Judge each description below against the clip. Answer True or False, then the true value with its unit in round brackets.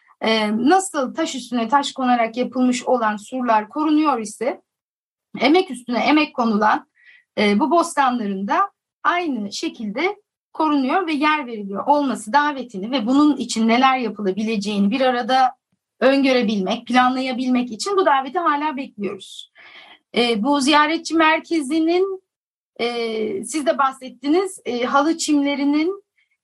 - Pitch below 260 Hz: False (265 Hz)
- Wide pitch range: False (4.9 semitones)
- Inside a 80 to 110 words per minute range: True (105 wpm)